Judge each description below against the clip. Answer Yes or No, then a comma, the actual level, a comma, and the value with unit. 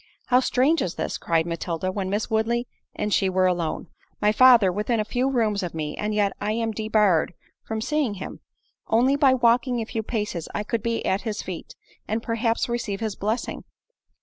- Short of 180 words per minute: No, average, 195 wpm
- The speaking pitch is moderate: No, high, 215 Hz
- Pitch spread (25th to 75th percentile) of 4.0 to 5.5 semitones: No, average, 3.5 semitones